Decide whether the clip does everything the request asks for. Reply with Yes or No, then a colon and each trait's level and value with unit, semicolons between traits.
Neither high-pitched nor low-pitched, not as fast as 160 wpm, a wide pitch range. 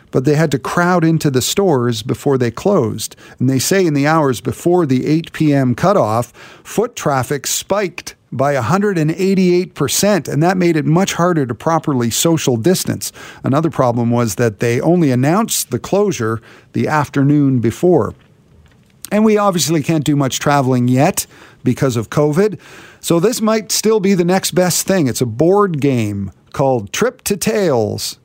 No: medium, 150 Hz; average, 165 wpm; wide, 6.0 semitones